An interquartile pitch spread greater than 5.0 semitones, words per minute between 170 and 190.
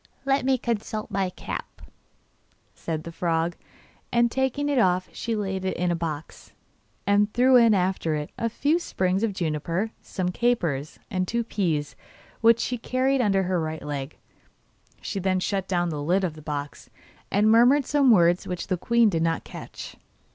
Yes: wide, 5.6 semitones; average, 175 wpm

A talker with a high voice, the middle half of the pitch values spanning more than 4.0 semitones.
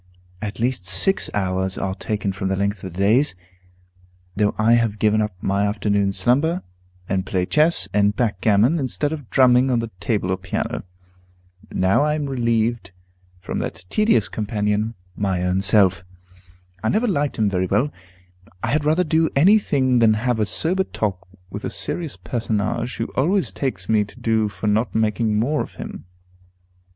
No: low, 110 Hz; average, 4.8 semitones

